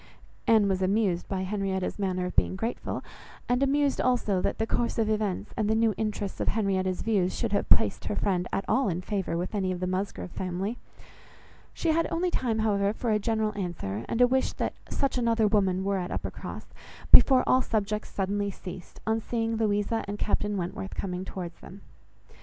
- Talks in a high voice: Yes, high, 205 Hz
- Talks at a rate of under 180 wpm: No, average, 195 wpm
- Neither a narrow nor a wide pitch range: Yes, average, 3.2 semitones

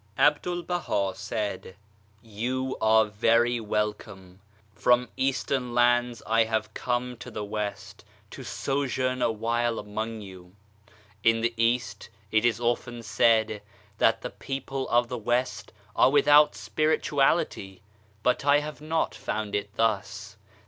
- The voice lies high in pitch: No, low, 115 Hz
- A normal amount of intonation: Yes, average, 3.1 semitones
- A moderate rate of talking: No, slow, 130 wpm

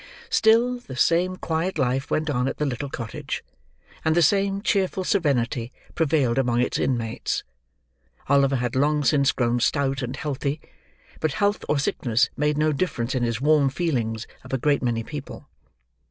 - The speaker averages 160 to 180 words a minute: Yes, average, 165 wpm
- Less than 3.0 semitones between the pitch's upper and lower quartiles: No, average, 4.2 semitones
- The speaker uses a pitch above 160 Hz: No, medium, 140 Hz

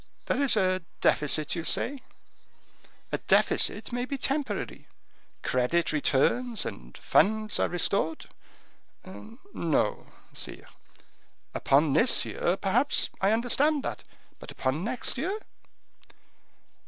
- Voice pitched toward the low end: No, high, 205 Hz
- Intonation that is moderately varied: No, wide, 8.3 semitones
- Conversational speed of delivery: No, slow, 105 wpm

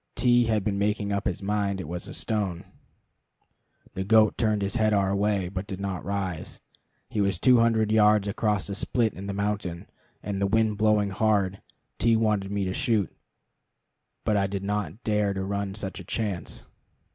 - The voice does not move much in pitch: Yes, narrow, 1.7 semitones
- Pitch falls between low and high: No, low, 100 Hz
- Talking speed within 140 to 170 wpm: No, average, 185 wpm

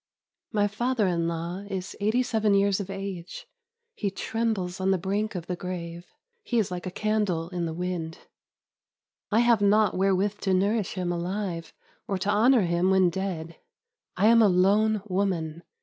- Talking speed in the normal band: Yes, average, 170 wpm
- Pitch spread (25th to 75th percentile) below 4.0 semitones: Yes, average, 2.8 semitones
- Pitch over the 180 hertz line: Yes, high, 190 Hz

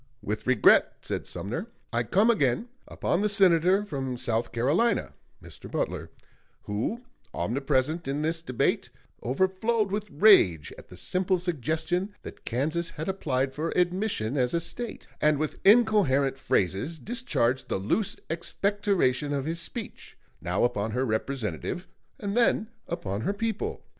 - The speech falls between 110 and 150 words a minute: Yes, average, 140 wpm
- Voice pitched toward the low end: No, medium, 160 Hz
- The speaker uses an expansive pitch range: Yes, wide, 7.7 semitones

